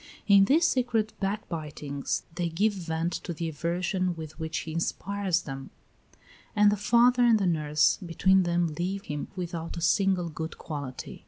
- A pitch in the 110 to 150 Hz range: No, medium, 175 Hz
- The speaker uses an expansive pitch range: No, average, 3.8 semitones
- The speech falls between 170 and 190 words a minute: No, average, 160 wpm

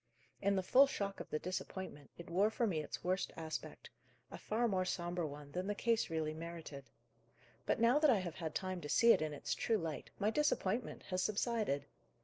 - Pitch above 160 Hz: Yes, medium, 185 Hz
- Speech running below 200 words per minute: No, fast, 205 wpm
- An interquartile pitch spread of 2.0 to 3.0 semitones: No, average, 5.2 semitones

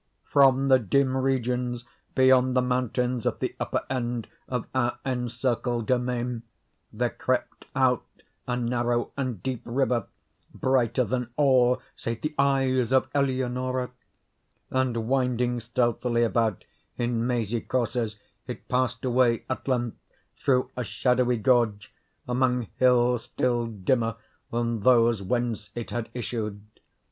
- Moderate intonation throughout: No, narrow, 1.5 semitones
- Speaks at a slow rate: Yes, slow, 125 wpm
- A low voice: Yes, low, 125 Hz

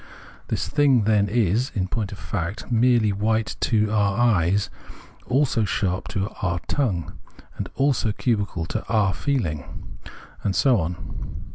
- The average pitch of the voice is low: Yes, low, 105 Hz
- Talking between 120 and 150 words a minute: Yes, average, 140 wpm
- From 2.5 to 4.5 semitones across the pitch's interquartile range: Yes, average, 4.0 semitones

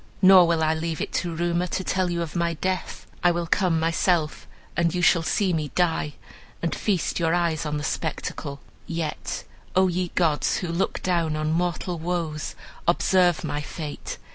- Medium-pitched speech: Yes, medium, 170 Hz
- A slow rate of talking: No, average, 180 wpm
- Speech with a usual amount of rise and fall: No, narrow, 1.9 semitones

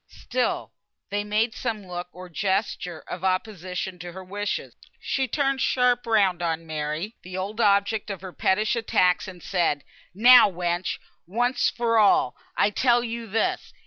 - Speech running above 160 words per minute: No, average, 155 wpm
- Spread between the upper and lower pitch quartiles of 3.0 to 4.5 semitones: Yes, average, 4.1 semitones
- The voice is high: Yes, high, 200 Hz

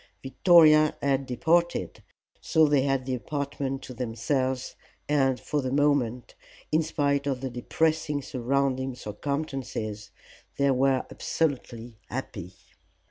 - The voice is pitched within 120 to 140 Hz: Yes, low, 135 Hz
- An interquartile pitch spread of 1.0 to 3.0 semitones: Yes, narrow, 2.4 semitones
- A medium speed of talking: No, slow, 115 wpm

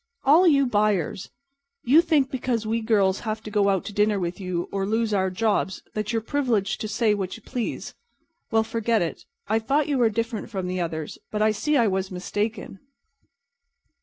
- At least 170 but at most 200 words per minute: Yes, average, 195 wpm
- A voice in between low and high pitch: No, high, 215 Hz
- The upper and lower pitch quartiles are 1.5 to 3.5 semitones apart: Yes, average, 3.1 semitones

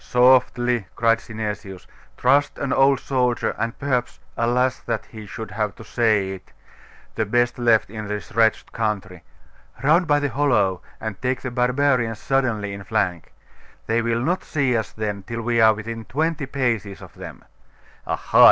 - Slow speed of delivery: No, average, 160 wpm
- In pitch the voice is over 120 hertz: No, low, 115 Hz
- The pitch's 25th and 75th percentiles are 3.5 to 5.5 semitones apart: No, average, 3.0 semitones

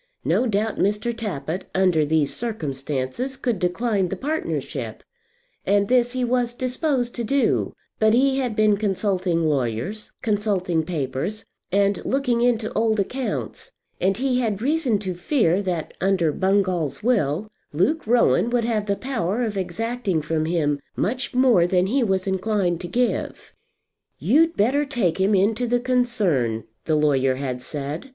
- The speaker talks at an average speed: Yes, average, 150 wpm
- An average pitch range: No, wide, 5.9 semitones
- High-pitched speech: Yes, high, 205 Hz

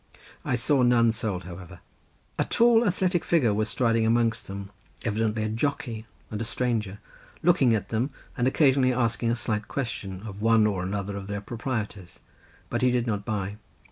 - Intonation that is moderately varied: Yes, average, 3.3 semitones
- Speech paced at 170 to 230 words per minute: Yes, average, 175 wpm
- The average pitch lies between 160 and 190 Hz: No, low, 115 Hz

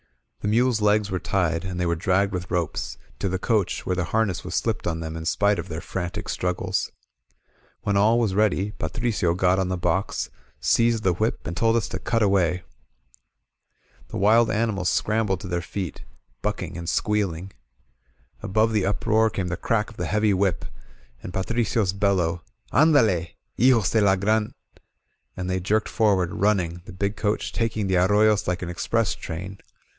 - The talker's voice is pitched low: Yes, low, 100 Hz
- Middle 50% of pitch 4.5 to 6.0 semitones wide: No, average, 3.2 semitones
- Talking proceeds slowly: No, average, 185 wpm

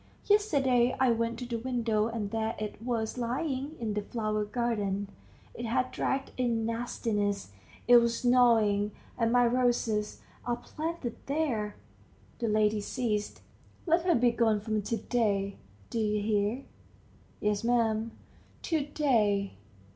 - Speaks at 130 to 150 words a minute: Yes, average, 140 wpm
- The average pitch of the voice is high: Yes, high, 230 Hz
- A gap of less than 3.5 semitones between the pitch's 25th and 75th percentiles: Yes, average, 2.7 semitones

